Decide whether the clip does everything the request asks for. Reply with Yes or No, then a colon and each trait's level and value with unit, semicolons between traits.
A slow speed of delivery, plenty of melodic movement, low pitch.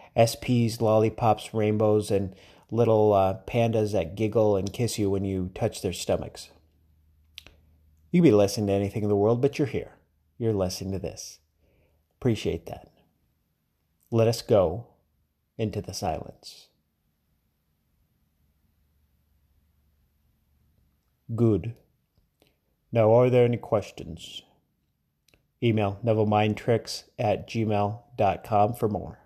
Yes: slow, 105 wpm; wide, 6.2 semitones; low, 100 Hz